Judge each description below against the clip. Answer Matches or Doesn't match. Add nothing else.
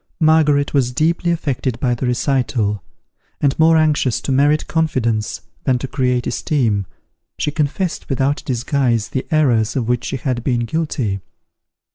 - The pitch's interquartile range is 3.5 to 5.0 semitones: Matches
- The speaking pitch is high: Doesn't match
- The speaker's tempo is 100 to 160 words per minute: Matches